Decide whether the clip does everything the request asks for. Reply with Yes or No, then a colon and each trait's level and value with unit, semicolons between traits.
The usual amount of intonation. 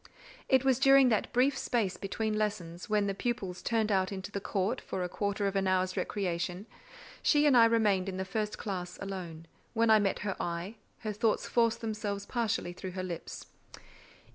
Yes: average, 3.3 semitones